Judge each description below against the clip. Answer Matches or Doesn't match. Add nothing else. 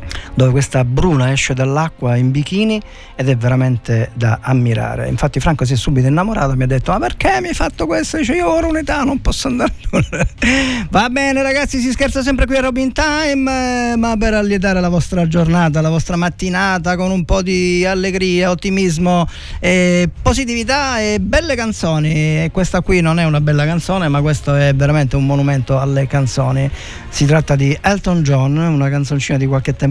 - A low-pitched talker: Doesn't match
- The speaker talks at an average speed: Doesn't match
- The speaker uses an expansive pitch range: Matches